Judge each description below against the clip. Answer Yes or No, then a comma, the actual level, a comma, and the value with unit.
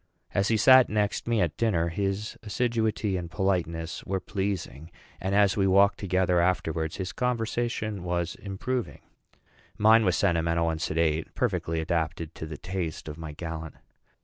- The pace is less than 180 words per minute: Yes, average, 150 wpm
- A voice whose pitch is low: Yes, very low, 95 Hz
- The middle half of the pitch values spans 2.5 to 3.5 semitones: No, average, 4.1 semitones